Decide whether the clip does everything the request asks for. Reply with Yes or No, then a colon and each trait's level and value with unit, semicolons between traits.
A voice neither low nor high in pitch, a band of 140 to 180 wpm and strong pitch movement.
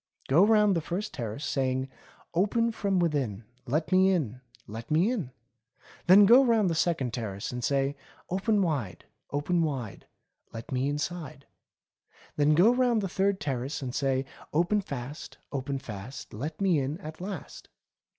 Yes: medium, 150 Hz; average, 160 wpm; wide, 6.4 semitones